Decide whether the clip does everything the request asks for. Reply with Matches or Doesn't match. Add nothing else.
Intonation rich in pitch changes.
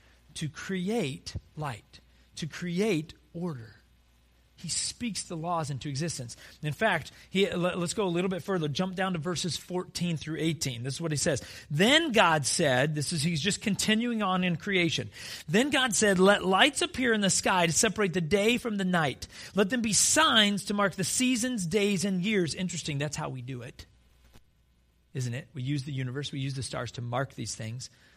Matches